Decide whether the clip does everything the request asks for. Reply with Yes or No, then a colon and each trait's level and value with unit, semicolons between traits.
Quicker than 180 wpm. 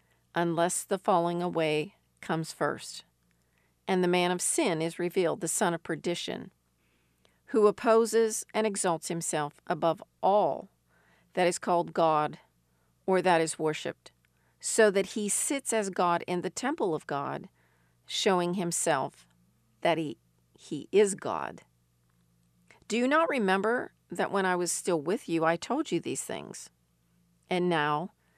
No: average, 145 wpm